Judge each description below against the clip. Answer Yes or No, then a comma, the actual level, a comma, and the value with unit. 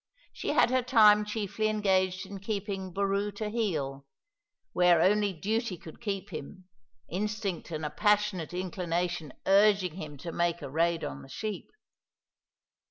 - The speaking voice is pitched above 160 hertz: Yes, high, 190 Hz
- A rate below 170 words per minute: Yes, average, 145 wpm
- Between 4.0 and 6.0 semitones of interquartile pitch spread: No, average, 3.5 semitones